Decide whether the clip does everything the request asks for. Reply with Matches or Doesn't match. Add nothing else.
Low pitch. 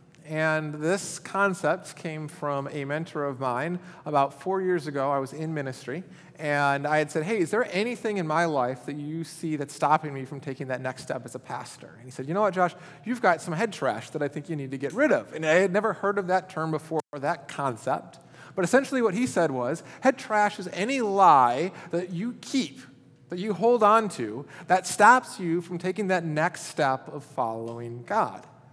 Doesn't match